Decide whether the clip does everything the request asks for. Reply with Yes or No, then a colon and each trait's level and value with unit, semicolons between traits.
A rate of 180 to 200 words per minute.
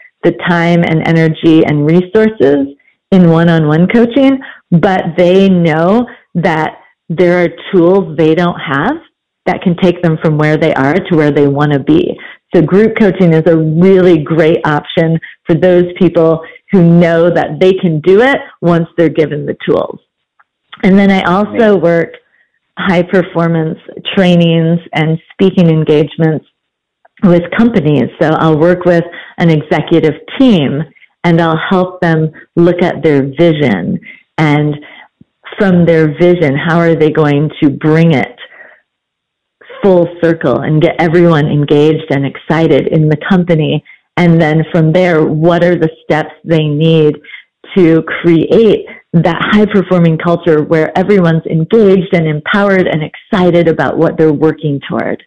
No: average, 150 wpm